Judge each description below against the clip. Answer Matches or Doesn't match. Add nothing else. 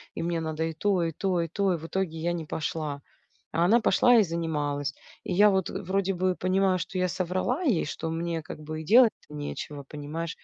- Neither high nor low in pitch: Matches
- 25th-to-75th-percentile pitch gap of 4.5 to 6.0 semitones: Doesn't match